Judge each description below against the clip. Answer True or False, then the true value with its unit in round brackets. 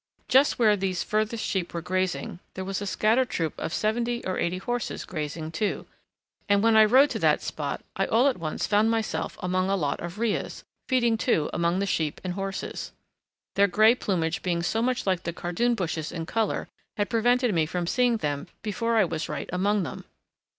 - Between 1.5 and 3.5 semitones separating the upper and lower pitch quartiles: False (4.7 semitones)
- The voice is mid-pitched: False (195 Hz)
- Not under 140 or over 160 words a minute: False (200 wpm)